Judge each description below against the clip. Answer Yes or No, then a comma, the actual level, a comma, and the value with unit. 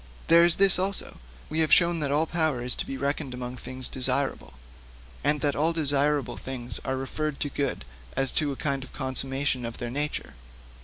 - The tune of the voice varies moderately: Yes, average, 3.0 semitones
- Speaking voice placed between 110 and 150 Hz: Yes, medium, 140 Hz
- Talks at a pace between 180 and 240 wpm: Yes, average, 195 wpm